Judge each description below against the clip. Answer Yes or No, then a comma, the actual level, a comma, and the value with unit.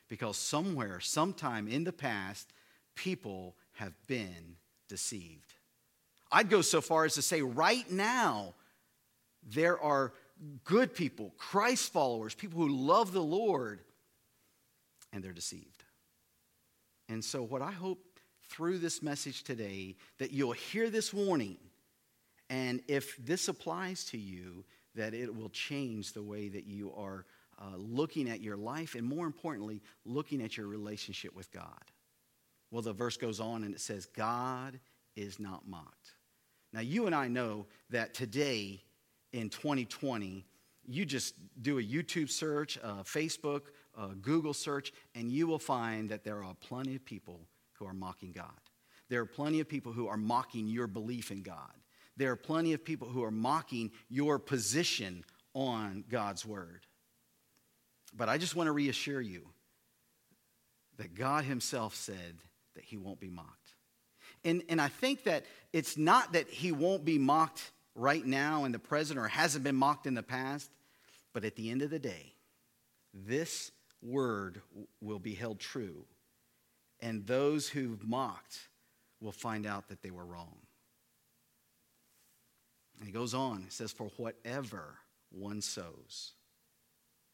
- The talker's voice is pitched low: Yes, low, 120 Hz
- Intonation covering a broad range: Yes, wide, 5.8 semitones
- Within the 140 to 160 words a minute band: Yes, average, 150 wpm